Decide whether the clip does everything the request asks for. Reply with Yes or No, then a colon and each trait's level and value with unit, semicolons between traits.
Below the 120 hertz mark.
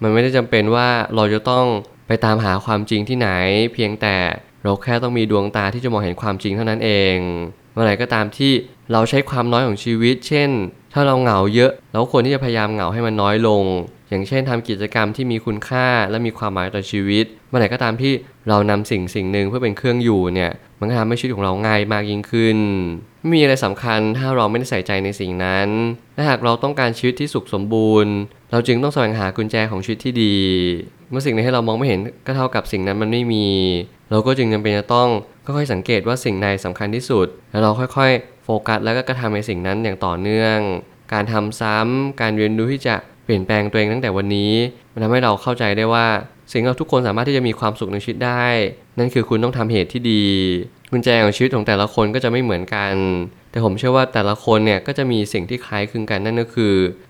Yes: low, 110 Hz